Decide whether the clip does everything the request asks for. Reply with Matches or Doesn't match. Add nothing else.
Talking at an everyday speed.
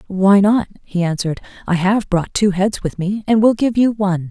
Doesn't match